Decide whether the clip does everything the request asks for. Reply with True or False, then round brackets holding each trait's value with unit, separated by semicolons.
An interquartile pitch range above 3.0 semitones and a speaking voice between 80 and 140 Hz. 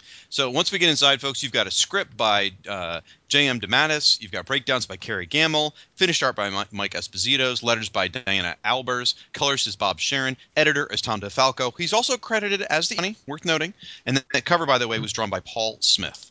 True (5.5 semitones; 135 Hz)